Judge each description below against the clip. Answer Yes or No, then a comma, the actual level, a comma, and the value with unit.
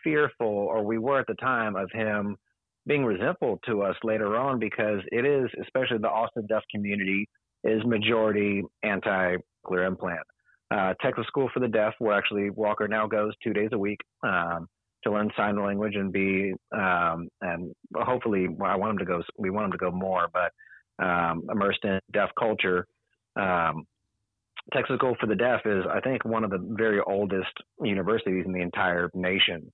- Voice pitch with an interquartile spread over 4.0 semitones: No, average, 2.8 semitones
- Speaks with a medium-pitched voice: No, low, 105 Hz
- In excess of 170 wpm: Yes, average, 180 wpm